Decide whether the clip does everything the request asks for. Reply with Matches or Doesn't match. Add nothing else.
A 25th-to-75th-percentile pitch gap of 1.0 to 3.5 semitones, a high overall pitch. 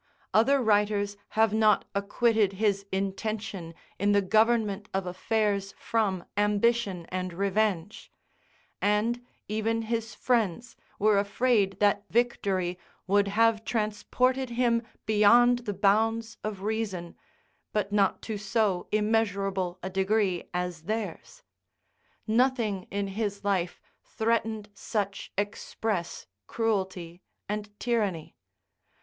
Matches